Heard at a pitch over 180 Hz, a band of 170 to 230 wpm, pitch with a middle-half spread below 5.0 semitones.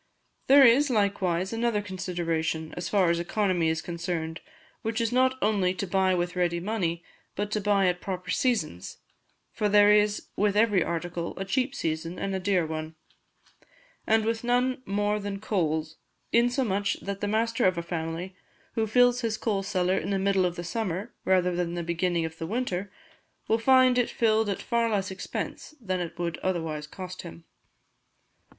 Yes: high, 190 Hz; average, 175 wpm; average, 4.1 semitones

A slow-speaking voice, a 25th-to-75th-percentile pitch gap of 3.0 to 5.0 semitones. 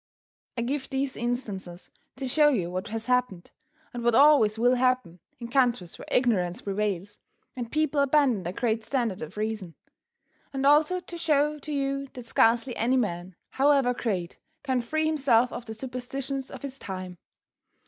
No: average, 165 wpm; average, 4.5 semitones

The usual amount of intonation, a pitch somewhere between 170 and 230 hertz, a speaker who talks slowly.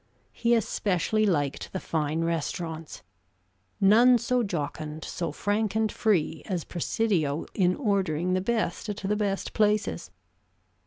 Yes: average, 4.9 semitones; high, 190 Hz; slow, 125 wpm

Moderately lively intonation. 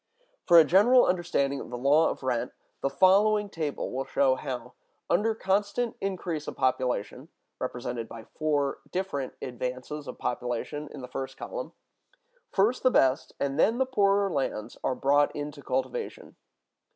No: wide, 7.0 semitones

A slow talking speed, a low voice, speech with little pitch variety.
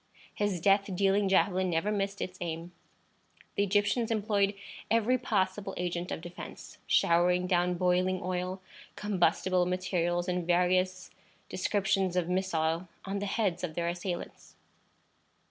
No: slow, 130 wpm; medium, 185 Hz; narrow, 2.0 semitones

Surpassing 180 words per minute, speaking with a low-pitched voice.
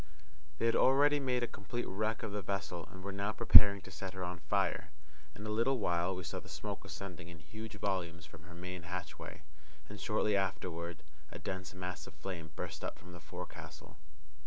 Yes: average, 200 wpm; very low, 95 Hz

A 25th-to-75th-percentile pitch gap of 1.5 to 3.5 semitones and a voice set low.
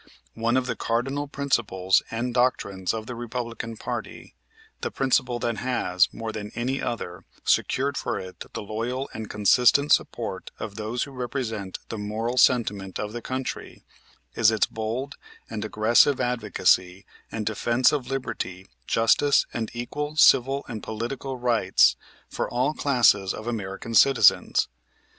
Yes: average, 3.0 semitones; low, 115 Hz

